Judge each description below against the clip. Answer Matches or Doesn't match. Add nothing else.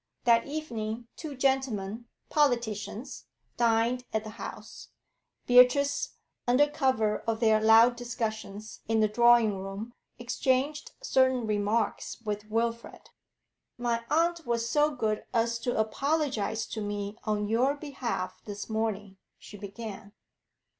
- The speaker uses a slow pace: Matches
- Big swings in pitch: Doesn't match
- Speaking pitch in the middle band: Doesn't match